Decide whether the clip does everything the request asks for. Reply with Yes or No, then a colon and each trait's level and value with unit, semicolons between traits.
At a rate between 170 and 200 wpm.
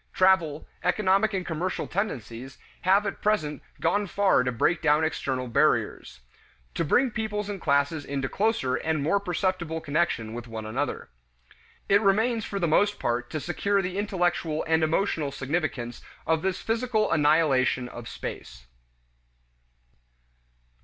No: average, 140 wpm